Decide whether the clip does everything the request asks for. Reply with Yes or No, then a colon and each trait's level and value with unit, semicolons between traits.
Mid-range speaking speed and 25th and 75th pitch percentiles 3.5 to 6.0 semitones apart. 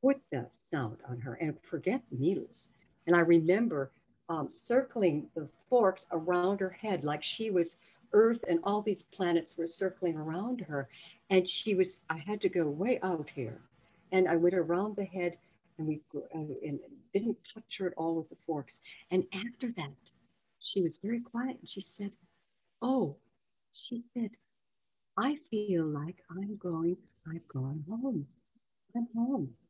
Yes: average, 165 wpm; average, 4.6 semitones